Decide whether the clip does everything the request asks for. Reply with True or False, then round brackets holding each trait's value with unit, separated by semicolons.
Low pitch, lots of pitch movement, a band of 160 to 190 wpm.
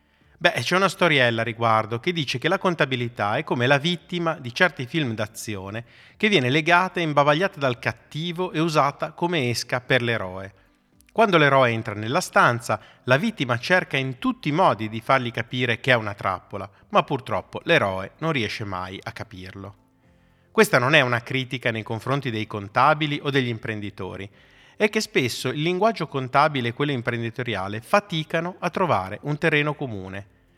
True (130 Hz; 6.6 semitones; 170 wpm)